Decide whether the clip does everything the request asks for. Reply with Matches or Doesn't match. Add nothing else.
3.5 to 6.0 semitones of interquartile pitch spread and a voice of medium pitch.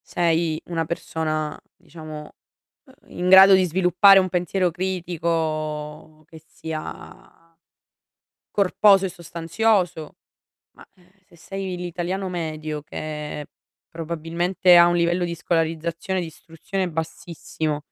Doesn't match